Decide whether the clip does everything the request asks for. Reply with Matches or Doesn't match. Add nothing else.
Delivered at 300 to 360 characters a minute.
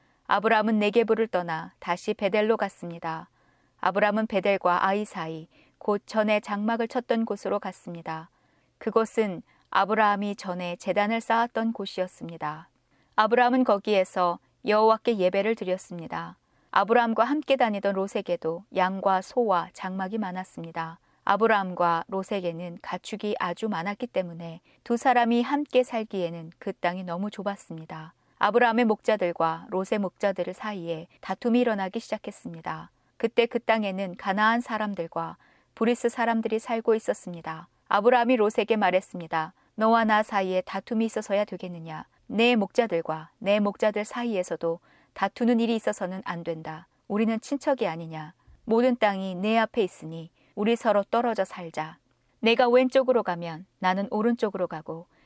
Matches